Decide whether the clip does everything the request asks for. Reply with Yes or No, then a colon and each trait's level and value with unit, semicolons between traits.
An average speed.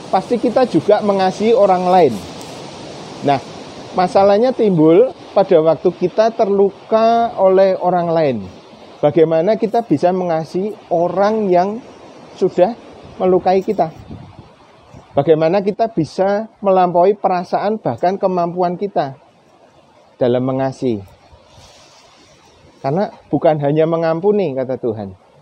Yes: average, 95 wpm